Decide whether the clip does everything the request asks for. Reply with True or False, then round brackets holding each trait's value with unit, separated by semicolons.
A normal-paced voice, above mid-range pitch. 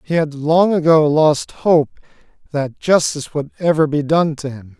False (175 wpm; 155 Hz)